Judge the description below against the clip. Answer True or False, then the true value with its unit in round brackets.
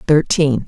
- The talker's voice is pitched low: False (145 Hz)